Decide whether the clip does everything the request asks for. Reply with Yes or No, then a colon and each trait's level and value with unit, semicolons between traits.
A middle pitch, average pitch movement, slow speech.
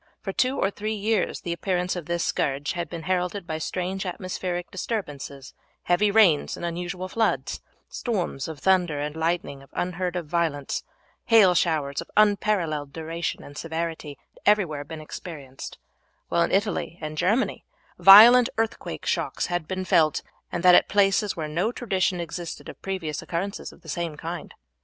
No: medium, 175 Hz; average, 3.5 semitones; average, 165 wpm